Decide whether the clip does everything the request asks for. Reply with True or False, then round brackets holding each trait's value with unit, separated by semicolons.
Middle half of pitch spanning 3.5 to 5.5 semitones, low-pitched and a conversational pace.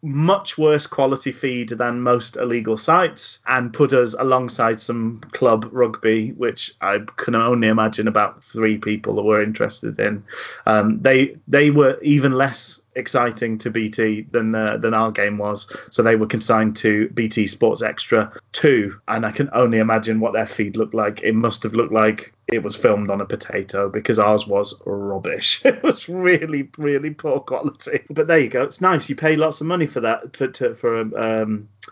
True (3.8 semitones; 115 Hz; 185 wpm)